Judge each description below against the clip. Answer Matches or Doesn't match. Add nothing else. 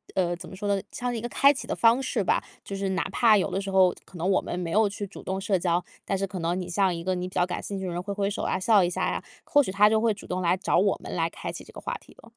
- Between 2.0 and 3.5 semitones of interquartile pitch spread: Matches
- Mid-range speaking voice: Doesn't match